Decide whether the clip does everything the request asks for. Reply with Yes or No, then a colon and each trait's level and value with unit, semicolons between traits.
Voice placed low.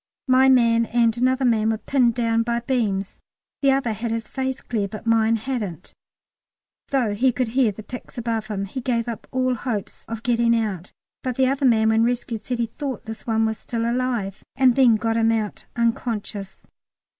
No: high, 230 Hz